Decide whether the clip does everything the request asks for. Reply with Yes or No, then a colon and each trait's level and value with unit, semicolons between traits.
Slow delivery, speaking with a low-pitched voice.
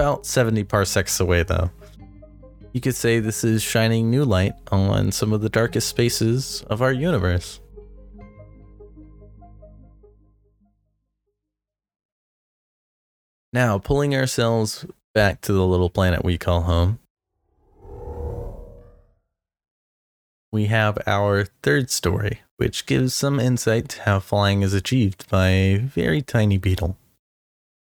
Yes: slow, 110 wpm; low, 105 Hz